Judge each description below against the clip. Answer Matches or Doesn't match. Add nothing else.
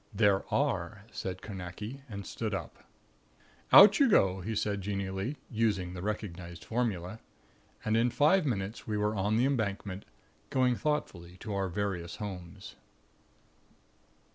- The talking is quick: Doesn't match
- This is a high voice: Doesn't match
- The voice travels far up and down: Doesn't match